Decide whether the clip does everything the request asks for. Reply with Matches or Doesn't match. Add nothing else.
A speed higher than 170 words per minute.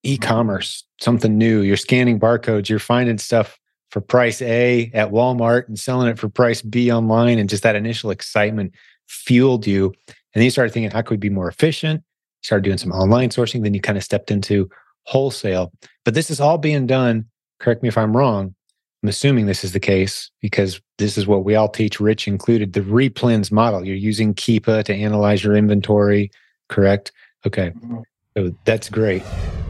Matches